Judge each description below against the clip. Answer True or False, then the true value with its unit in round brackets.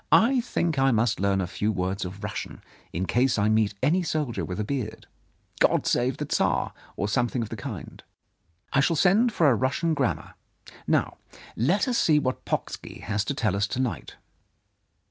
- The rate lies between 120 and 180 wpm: False (200 wpm)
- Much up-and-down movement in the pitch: True (6.5 semitones)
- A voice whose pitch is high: False (120 Hz)